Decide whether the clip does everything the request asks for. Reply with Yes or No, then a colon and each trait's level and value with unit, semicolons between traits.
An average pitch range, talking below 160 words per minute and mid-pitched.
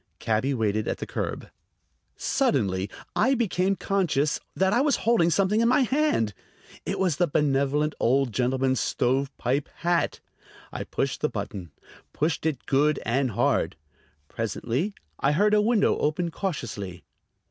No: wide, 7.5 semitones; average, 140 wpm; medium, 150 Hz